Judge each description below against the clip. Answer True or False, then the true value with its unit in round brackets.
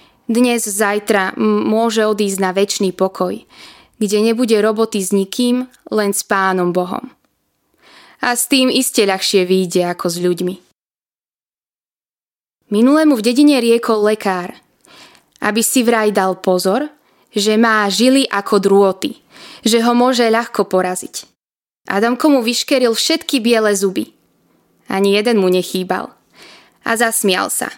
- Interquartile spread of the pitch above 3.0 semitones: True (3.8 semitones)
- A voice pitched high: True (215 Hz)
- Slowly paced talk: False (125 wpm)